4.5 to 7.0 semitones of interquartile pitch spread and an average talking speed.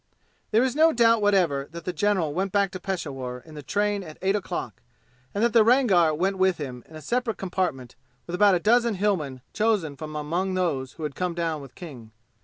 No: average, 5.2 semitones; fast, 210 wpm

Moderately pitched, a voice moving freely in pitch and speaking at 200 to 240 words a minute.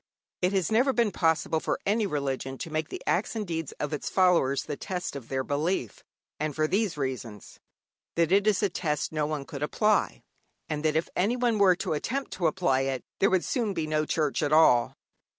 No: medium, 160 Hz; average, 4.9 semitones; fast, 205 wpm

